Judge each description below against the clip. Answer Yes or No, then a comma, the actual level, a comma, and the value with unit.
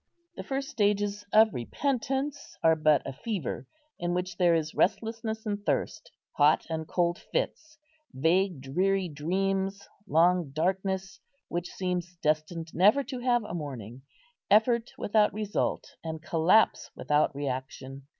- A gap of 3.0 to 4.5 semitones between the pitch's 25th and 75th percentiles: No, average, 5.1 semitones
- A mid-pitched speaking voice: Yes, medium, 180 Hz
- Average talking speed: No, slow, 130 wpm